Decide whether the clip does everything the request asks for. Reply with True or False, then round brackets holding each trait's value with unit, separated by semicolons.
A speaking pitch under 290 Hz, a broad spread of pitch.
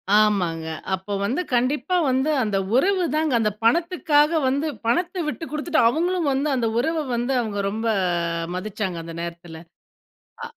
True (255 Hz; 7.1 semitones)